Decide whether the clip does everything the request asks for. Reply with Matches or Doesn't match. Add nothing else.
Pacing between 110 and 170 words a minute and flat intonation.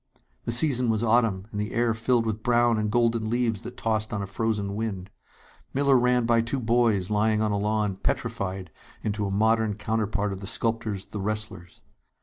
Doesn't match